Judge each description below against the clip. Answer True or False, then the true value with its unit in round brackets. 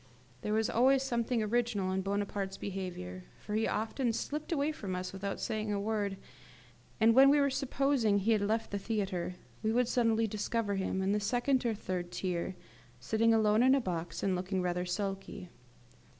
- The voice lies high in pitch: True (210 Hz)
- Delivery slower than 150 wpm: False (180 wpm)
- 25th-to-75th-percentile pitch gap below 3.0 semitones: False (3.4 semitones)